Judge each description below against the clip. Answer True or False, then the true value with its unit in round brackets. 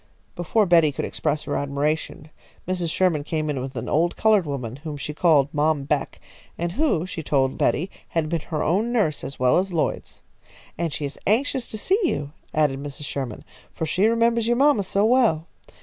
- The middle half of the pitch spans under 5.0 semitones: False (5.4 semitones)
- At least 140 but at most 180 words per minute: False (195 wpm)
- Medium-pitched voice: True (160 Hz)